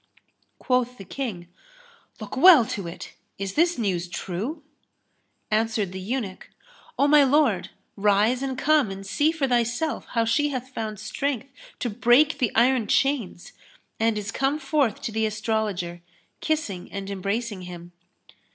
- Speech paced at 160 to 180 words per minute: No, average, 145 wpm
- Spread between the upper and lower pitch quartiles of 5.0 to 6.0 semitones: Yes, wide, 5.5 semitones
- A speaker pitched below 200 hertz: No, high, 230 Hz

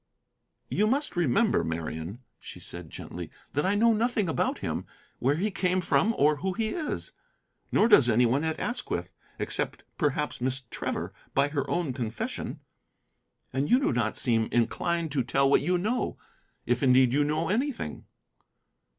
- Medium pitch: Yes, medium, 150 Hz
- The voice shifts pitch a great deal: Yes, wide, 8.1 semitones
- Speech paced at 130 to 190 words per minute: Yes, average, 160 wpm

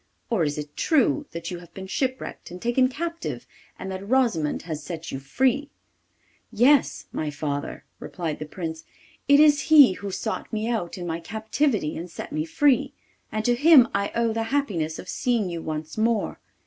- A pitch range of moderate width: No, wide, 7.8 semitones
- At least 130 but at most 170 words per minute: No, average, 185 wpm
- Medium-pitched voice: No, high, 210 Hz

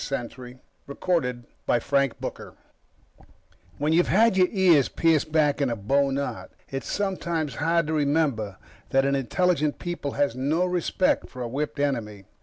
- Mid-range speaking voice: Yes, medium, 145 Hz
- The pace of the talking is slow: Yes, slow, 130 wpm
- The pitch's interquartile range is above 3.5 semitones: Yes, average, 4.2 semitones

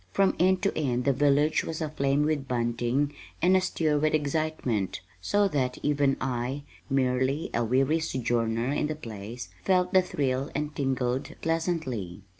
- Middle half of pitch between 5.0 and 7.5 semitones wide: No, average, 3.7 semitones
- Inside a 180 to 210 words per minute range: No, average, 150 wpm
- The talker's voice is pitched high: No, medium, 140 Hz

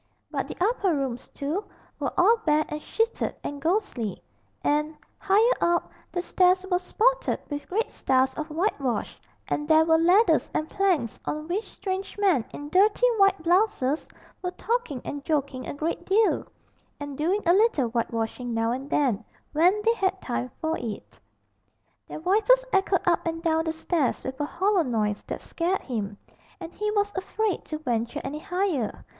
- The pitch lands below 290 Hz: No, very high, 330 Hz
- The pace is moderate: Yes, average, 170 wpm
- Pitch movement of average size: No, wide, 5.7 semitones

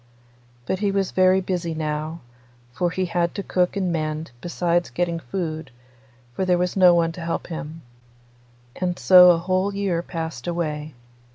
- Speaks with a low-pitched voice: No, medium, 175 Hz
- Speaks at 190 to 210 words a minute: No, average, 165 wpm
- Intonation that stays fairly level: Yes, narrow, 2.2 semitones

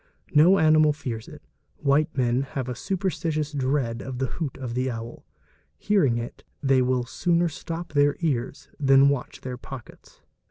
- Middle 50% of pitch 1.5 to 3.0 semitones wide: No, average, 3.6 semitones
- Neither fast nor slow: Yes, average, 160 wpm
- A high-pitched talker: No, low, 135 Hz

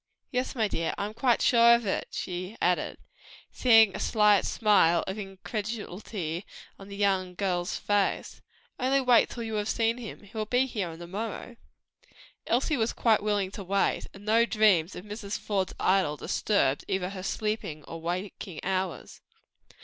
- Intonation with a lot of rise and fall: No, average, 3.3 semitones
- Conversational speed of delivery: Yes, average, 165 wpm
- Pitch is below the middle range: No, high, 205 Hz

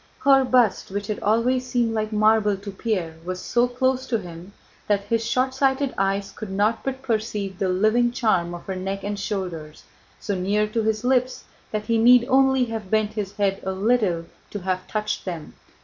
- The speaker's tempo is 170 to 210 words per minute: Yes, average, 190 wpm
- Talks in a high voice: Yes, high, 215 Hz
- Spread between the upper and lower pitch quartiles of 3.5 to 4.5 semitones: Yes, average, 3.8 semitones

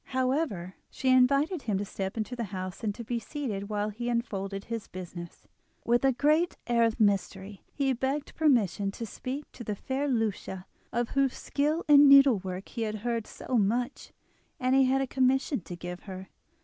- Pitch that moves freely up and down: No, average, 5.0 semitones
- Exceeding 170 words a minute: Yes, average, 180 wpm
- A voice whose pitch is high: Yes, high, 235 Hz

